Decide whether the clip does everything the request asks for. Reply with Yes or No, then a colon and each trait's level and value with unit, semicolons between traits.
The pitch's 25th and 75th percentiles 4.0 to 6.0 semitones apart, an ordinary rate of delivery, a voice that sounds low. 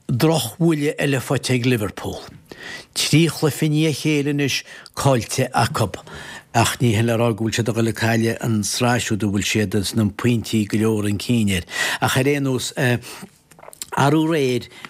Yes: average, 4.3 semitones; average, 150 wpm; low, 120 Hz